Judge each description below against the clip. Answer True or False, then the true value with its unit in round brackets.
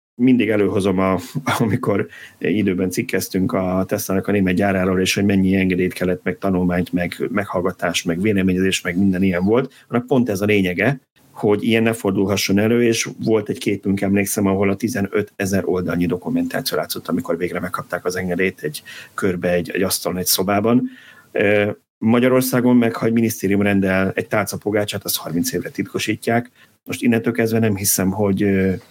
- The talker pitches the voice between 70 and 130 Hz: True (100 Hz)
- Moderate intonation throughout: True (3.0 semitones)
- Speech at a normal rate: False (160 wpm)